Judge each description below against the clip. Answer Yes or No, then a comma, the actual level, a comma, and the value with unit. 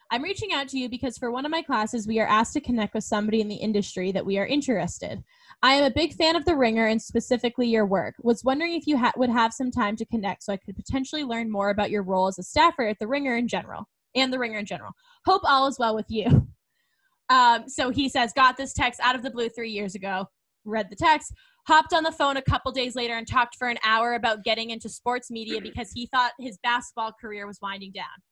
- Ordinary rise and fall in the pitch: Yes, average, 3.6 semitones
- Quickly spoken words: Yes, fast, 255 wpm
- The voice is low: No, high, 240 Hz